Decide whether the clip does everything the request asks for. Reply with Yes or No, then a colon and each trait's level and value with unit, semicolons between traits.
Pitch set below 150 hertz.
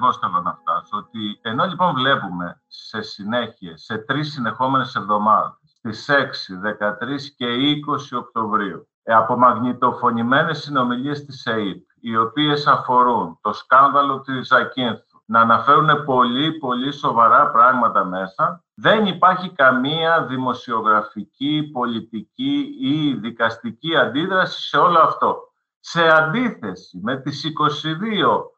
Yes: low, 135 Hz